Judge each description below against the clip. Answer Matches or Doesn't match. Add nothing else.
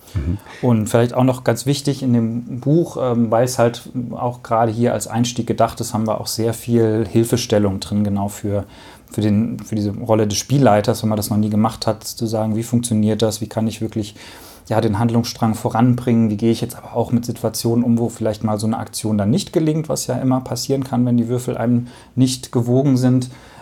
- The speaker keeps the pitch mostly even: Matches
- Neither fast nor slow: Doesn't match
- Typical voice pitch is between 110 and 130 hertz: Matches